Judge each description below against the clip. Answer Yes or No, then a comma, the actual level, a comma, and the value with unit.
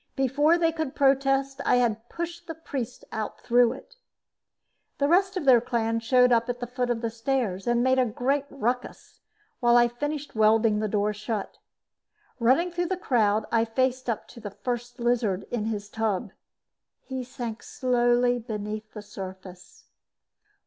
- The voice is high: Yes, high, 240 Hz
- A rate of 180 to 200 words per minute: No, average, 165 wpm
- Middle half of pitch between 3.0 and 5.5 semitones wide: Yes, average, 3.3 semitones